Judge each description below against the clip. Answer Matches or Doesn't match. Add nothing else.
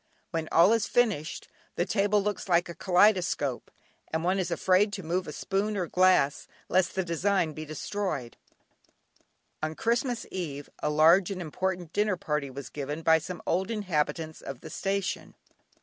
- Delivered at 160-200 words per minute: Matches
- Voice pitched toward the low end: Doesn't match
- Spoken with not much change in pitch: Doesn't match